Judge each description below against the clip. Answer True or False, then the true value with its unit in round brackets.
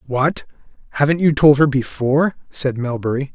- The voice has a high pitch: False (140 Hz)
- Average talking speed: True (145 wpm)